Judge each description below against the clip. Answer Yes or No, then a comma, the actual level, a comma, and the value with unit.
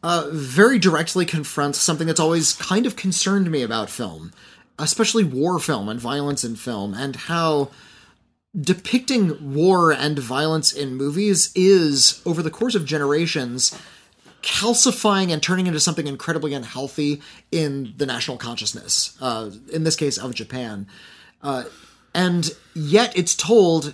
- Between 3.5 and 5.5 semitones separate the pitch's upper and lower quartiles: Yes, average, 4.7 semitones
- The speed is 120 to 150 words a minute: Yes, average, 140 wpm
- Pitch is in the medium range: Yes, medium, 155 Hz